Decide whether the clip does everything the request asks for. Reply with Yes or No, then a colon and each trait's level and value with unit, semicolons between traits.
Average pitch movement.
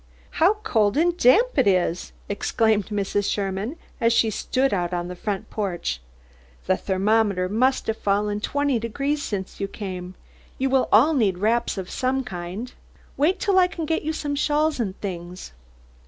No: wide, 6.2 semitones